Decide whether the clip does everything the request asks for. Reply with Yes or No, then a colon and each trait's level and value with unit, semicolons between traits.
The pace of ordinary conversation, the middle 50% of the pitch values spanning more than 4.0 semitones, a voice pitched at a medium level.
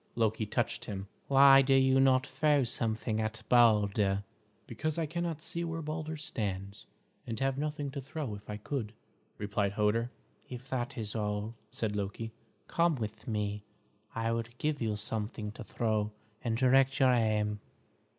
No: average, 160 wpm; average, 4.4 semitones; low, 115 Hz